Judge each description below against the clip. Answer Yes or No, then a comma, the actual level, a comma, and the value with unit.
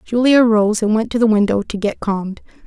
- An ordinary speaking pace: No, fast, 225 wpm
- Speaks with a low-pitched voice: No, high, 215 Hz